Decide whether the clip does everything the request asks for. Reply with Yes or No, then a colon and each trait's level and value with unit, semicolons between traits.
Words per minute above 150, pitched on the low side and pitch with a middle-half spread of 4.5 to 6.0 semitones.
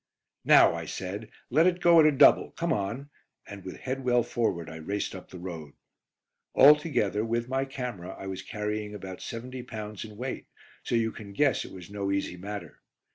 Yes: average, 190 wpm; low, 110 Hz; average, 4.8 semitones